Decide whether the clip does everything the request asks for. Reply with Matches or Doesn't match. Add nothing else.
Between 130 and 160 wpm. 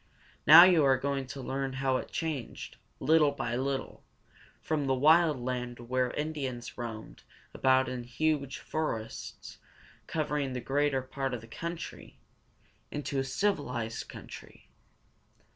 Matches